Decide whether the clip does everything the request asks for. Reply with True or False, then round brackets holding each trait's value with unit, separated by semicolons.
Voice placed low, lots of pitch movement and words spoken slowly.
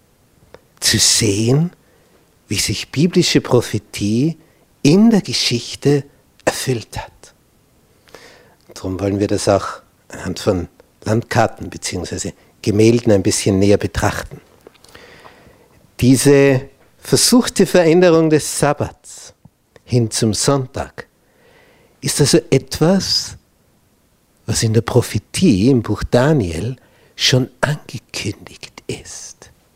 True (120 Hz; 5.7 semitones; 95 wpm)